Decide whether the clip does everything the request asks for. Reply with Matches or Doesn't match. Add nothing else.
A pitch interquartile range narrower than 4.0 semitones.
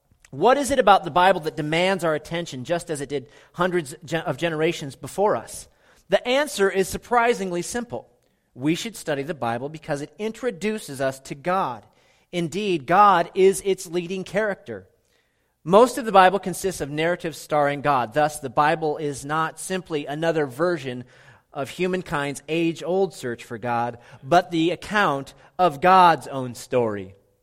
Doesn't match